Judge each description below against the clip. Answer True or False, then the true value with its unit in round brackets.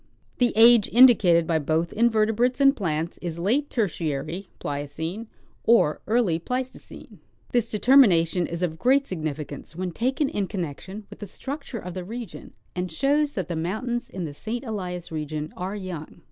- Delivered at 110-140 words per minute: False (160 wpm)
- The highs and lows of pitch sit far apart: True (6.4 semitones)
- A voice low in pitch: False (190 Hz)